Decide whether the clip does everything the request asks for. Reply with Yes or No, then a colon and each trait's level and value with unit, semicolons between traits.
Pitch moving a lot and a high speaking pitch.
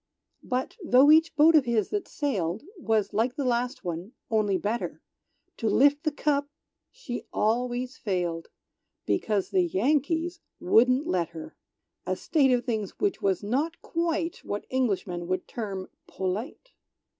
Yes: wide, 6.6 semitones; high, 240 Hz